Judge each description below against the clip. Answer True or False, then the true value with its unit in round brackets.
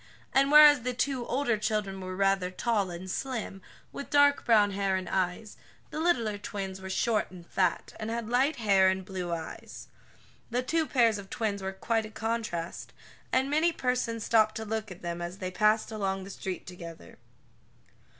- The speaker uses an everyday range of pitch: True (3.9 semitones)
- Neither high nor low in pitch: False (215 Hz)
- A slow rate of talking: False (180 wpm)